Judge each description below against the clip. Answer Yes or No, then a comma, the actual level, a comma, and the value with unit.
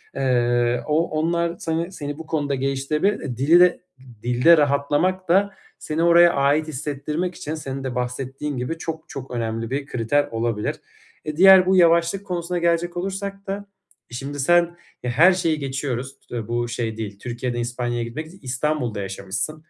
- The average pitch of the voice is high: No, medium, 145 Hz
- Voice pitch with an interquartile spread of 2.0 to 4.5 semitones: No, wide, 5.5 semitones